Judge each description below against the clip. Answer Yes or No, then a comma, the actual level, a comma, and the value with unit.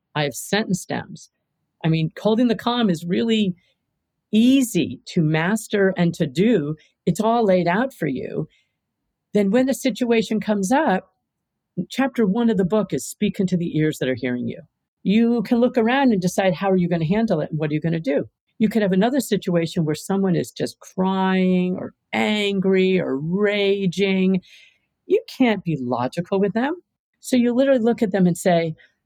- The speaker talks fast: No, average, 190 wpm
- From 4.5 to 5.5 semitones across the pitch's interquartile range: Yes, average, 4.8 semitones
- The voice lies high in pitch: Yes, high, 195 Hz